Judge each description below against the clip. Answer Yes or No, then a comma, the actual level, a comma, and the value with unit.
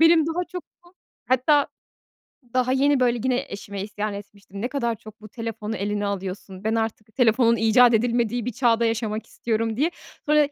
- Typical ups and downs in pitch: Yes, average, 3.2 semitones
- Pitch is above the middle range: Yes, high, 230 Hz